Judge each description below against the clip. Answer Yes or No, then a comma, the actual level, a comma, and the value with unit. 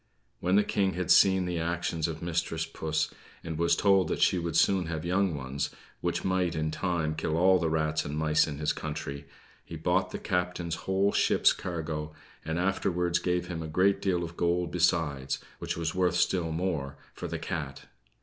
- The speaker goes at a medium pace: Yes, average, 190 wpm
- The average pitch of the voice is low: Yes, very low, 85 Hz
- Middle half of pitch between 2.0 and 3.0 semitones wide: Yes, narrow, 2.4 semitones